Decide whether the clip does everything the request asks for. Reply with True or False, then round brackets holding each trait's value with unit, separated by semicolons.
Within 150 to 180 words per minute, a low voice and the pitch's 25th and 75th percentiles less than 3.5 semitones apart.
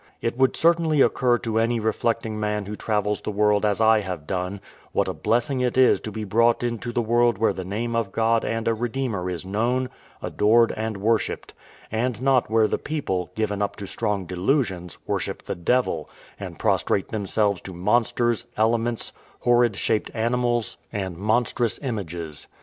True (170 wpm; 110 Hz; 2.7 semitones)